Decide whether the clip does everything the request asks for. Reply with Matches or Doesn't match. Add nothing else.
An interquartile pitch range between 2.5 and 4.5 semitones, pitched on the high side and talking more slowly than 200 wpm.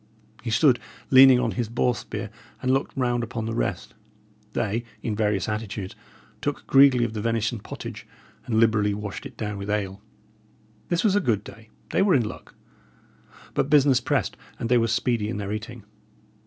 Doesn't match